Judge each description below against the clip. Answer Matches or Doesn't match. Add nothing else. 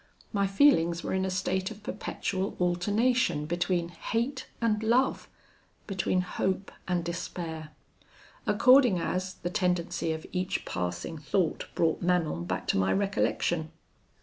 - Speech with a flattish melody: Doesn't match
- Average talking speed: Doesn't match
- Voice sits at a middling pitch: Matches